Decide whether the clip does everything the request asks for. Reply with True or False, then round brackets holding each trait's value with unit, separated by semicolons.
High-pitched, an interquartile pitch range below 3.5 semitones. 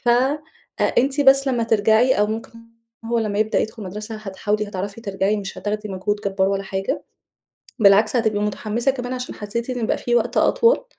True (215 Hz; 2.8 semitones)